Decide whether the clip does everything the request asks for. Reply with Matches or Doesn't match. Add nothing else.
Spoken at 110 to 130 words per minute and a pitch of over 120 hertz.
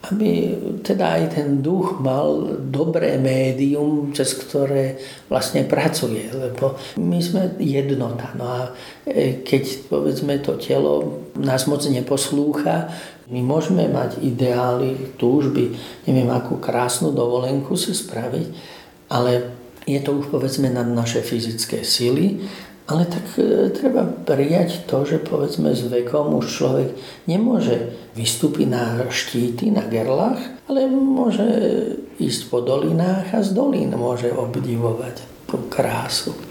Matches